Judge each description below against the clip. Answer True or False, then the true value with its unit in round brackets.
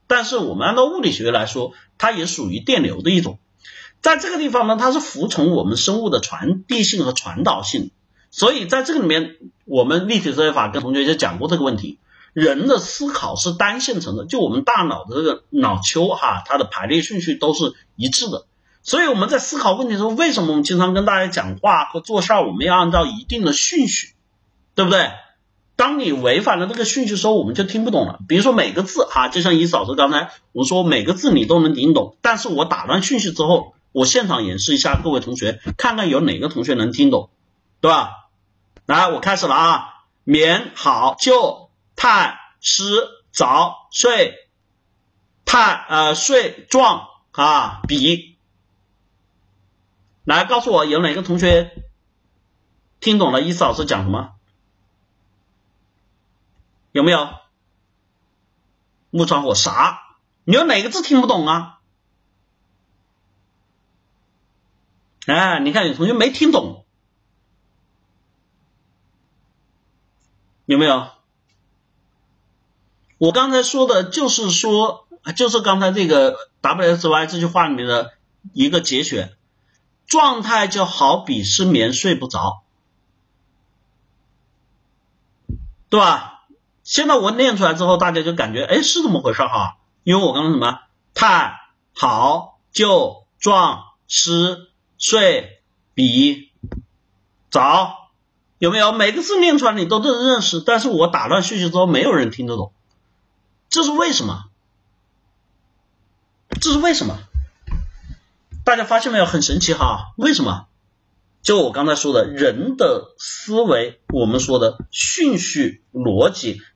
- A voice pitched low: False (175 Hz)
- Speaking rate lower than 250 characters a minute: True (220 characters per minute)